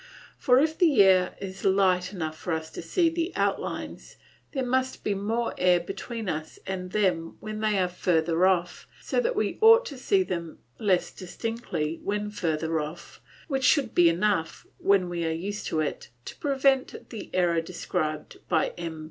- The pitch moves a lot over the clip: Yes, wide, 5.8 semitones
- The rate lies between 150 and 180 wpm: Yes, average, 175 wpm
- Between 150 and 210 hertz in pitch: Yes, high, 190 Hz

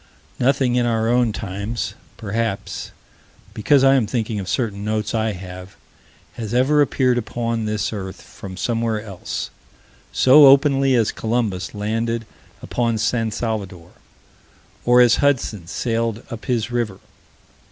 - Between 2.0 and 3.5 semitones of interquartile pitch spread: Yes, average, 2.7 semitones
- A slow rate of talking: Yes, slow, 130 wpm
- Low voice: Yes, low, 115 Hz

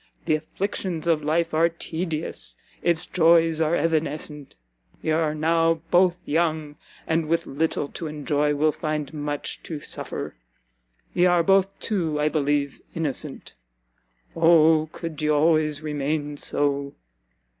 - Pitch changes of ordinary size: No, narrow, 1.8 semitones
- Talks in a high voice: No, medium, 155 Hz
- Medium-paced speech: No, slow, 130 wpm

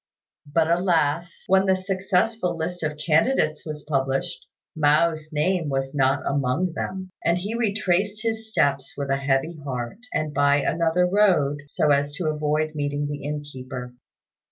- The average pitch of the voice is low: No, medium, 155 Hz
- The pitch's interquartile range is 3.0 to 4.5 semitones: Yes, average, 3.9 semitones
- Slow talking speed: No, average, 150 wpm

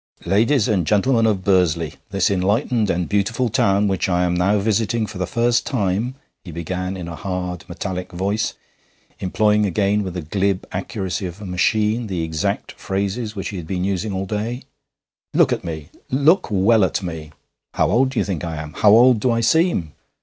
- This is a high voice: No, low, 100 Hz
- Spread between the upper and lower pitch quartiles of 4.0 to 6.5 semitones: No, average, 3.4 semitones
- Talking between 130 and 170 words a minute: No, average, 190 wpm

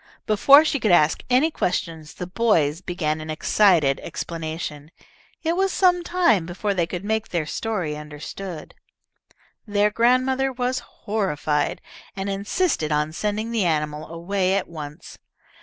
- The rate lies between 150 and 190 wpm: No, average, 140 wpm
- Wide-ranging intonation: Yes, wide, 6.6 semitones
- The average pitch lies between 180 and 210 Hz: Yes, high, 190 Hz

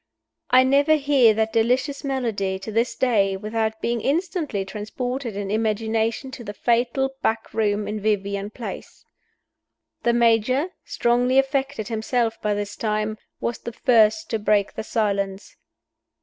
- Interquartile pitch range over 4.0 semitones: No, average, 3.3 semitones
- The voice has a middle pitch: No, high, 225 Hz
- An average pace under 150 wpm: Yes, average, 140 wpm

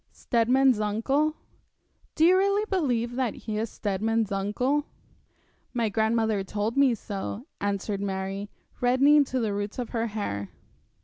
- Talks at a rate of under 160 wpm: Yes, slow, 135 wpm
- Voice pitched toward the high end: Yes, high, 225 Hz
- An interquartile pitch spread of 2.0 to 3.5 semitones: No, average, 4.2 semitones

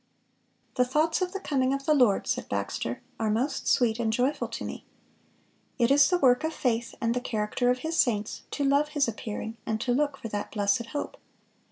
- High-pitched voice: Yes, very high, 250 Hz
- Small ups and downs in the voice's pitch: No, average, 4.2 semitones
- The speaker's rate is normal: No, fast, 210 wpm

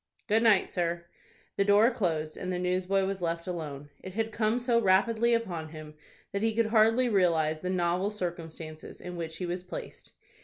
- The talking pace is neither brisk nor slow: Yes, average, 185 wpm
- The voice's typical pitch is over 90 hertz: Yes, medium, 185 Hz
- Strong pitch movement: No, average, 4.4 semitones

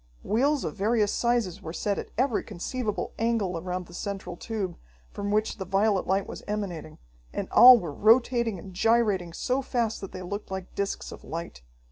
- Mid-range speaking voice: No, high, 205 Hz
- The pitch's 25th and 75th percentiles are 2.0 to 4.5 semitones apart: Yes, average, 3.9 semitones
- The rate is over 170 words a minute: Yes, average, 180 wpm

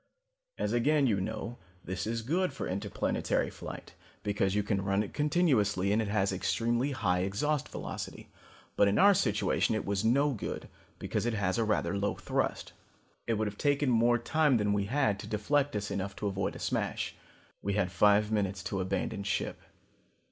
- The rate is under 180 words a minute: No, average, 185 wpm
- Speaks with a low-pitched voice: Yes, low, 105 Hz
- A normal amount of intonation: Yes, average, 3.5 semitones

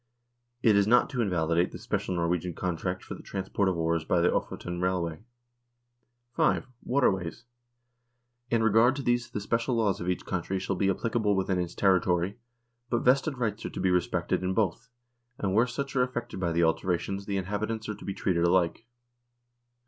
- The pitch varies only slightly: No, average, 4.3 semitones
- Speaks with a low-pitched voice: Yes, very low, 95 Hz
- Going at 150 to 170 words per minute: No, average, 180 wpm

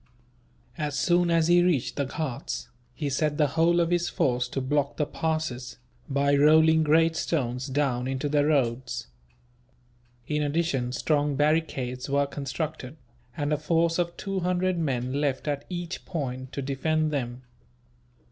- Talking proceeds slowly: No, average, 150 wpm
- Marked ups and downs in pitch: No, average, 3.4 semitones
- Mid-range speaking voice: Yes, medium, 145 Hz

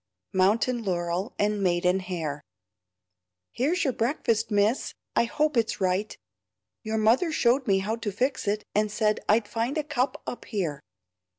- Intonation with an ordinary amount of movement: Yes, average, 4.2 semitones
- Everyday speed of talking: Yes, average, 155 wpm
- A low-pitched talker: No, high, 215 Hz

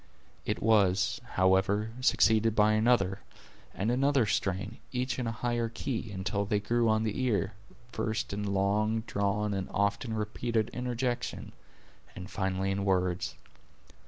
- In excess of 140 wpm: No, slow, 135 wpm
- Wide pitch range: No, average, 2.8 semitones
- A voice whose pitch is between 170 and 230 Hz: No, low, 105 Hz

